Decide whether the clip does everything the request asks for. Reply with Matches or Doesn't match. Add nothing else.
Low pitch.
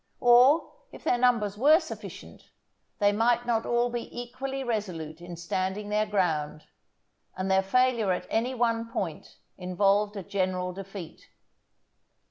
Doesn't match